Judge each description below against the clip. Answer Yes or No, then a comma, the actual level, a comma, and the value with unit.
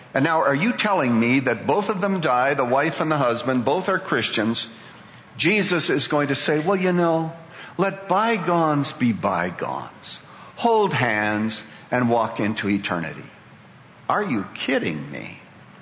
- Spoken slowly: No, average, 155 wpm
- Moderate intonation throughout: No, wide, 8.5 semitones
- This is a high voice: No, medium, 150 Hz